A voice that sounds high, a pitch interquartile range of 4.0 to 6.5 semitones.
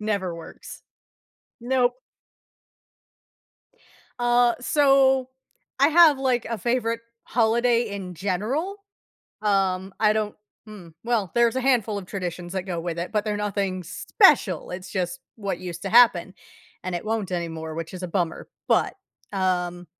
Yes: high, 205 Hz; average, 4.9 semitones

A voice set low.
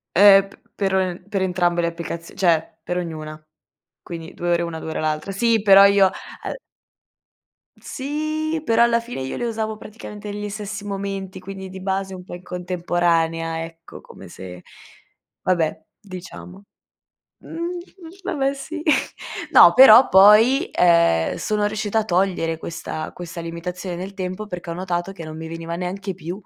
No: medium, 185 Hz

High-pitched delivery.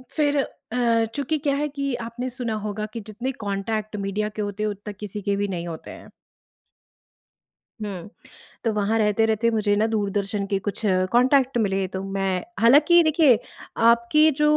Yes: high, 220 Hz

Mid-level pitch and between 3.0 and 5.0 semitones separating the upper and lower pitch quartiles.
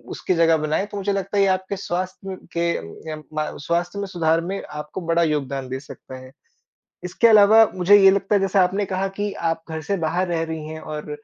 Yes: medium, 175 Hz; average, 3.6 semitones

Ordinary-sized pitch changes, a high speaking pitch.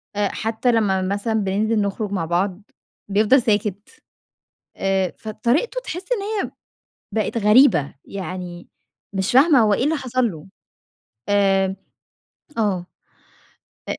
Yes: average, 3.3 semitones; high, 205 Hz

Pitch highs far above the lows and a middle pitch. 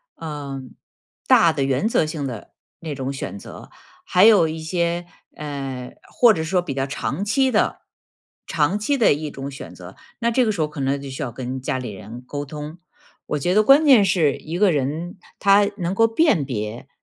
Yes: wide, 6.2 semitones; medium, 155 Hz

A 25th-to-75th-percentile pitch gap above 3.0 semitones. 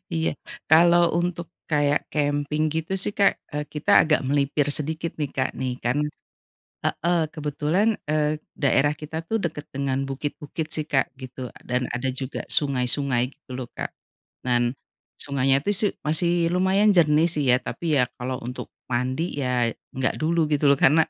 Yes: average, 3.5 semitones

